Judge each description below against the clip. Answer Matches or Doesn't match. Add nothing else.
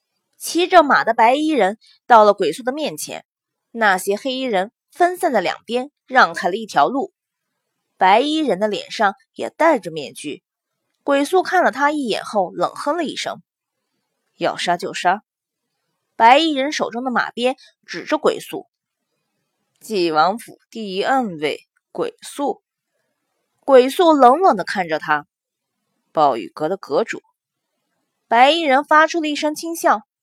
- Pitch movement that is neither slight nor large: Doesn't match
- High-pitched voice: Matches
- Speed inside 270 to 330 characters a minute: Doesn't match